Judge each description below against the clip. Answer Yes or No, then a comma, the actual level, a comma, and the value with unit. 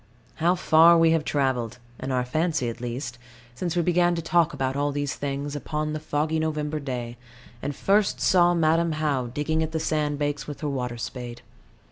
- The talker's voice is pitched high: No, medium, 150 Hz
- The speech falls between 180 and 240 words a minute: Yes, average, 190 wpm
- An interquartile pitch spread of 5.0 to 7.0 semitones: No, average, 3.4 semitones